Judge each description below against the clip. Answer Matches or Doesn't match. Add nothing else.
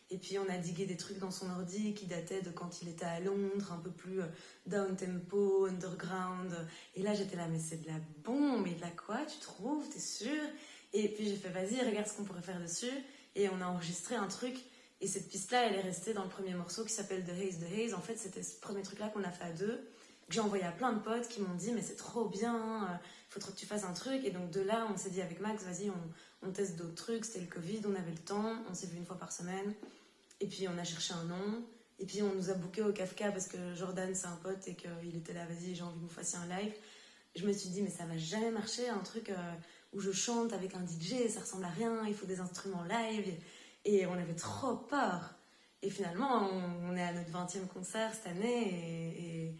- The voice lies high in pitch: Matches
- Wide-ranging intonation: Doesn't match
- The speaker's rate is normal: Doesn't match